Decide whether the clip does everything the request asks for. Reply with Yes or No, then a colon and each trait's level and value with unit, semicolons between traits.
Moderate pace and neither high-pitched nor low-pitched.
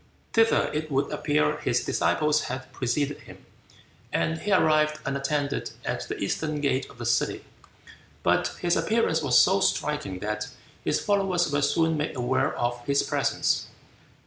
Yes: average, 150 wpm; medium, 150 Hz